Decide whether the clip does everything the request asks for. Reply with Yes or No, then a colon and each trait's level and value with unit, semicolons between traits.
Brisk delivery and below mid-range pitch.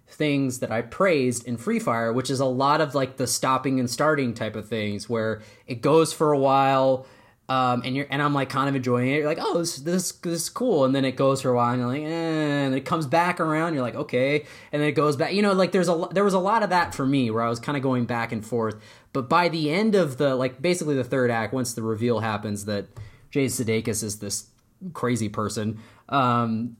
Yes: fast, 255 wpm; low, 130 Hz